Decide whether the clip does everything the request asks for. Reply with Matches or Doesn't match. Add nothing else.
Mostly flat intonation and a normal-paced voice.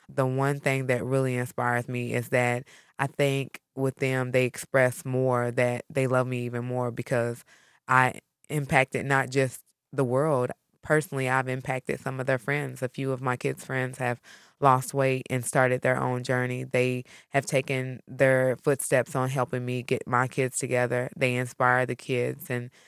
Matches